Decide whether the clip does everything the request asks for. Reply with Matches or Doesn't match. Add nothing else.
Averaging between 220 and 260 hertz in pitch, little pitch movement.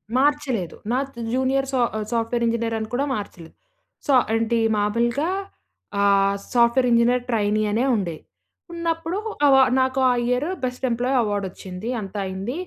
Doesn't match